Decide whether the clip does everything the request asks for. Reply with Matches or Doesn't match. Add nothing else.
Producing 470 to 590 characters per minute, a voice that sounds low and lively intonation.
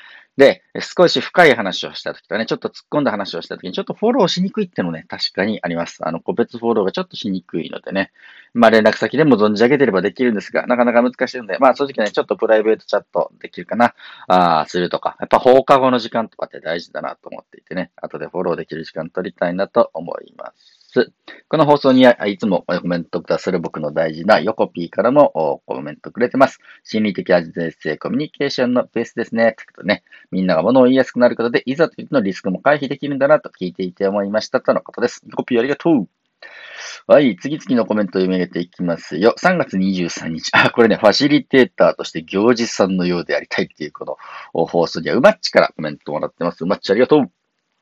Matches